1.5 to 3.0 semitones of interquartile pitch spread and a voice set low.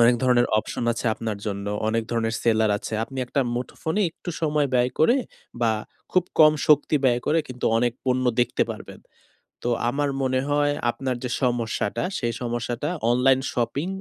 No: average, 3.4 semitones; low, 125 Hz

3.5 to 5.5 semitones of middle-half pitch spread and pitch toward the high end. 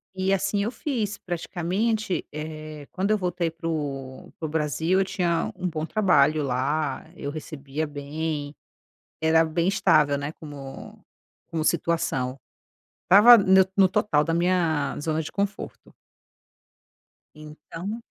No: average, 3.9 semitones; medium, 160 Hz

